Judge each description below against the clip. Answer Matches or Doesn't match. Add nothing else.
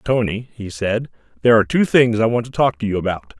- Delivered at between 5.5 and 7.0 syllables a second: Matches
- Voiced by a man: Matches